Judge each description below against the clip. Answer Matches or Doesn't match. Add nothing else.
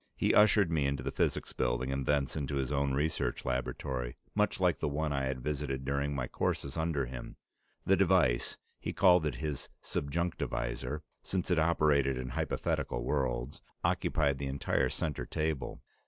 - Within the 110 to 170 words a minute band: Matches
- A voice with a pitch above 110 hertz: Doesn't match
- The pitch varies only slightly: Doesn't match